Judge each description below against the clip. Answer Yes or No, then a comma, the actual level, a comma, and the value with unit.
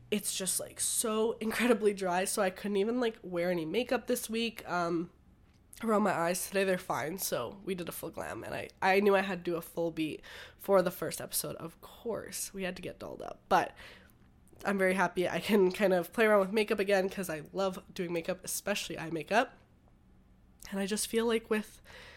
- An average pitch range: Yes, average, 3.3 semitones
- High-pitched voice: Yes, high, 195 Hz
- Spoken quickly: Yes, fast, 215 wpm